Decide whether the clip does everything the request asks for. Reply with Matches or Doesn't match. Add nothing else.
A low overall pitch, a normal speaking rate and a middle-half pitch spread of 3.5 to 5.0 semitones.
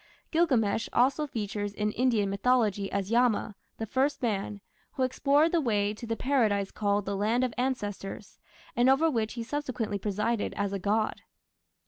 Doesn't match